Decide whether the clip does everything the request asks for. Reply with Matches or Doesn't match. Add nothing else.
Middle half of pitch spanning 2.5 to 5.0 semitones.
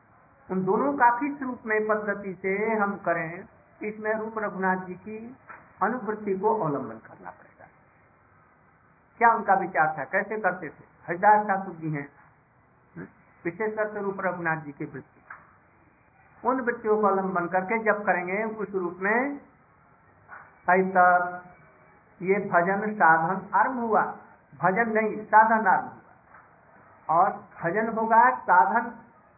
Matches